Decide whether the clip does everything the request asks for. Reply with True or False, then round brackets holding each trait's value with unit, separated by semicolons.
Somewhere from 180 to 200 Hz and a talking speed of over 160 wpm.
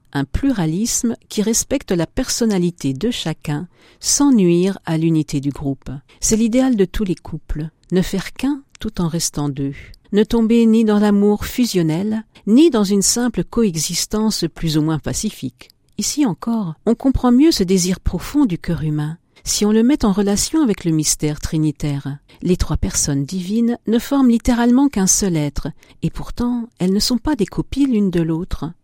True (190 Hz; 175 wpm)